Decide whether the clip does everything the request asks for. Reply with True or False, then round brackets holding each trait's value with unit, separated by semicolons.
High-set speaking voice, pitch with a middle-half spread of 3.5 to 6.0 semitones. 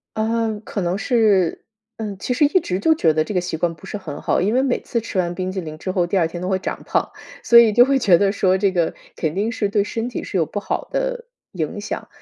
True (200 Hz; 4.4 semitones)